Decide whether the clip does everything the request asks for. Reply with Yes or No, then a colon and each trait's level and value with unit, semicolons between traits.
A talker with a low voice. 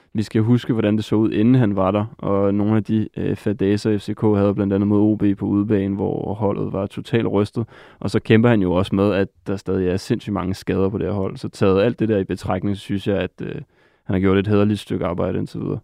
Yes: low, 100 Hz